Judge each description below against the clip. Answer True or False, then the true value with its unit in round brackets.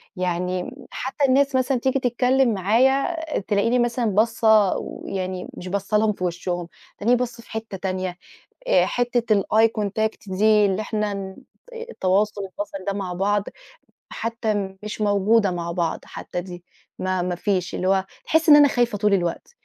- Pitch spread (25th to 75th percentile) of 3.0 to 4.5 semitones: True (4.0 semitones)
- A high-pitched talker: True (205 Hz)